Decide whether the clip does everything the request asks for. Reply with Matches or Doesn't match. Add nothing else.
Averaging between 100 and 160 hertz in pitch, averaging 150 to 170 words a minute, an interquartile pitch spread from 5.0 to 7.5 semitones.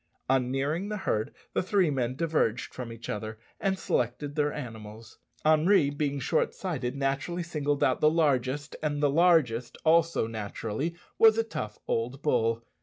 Matches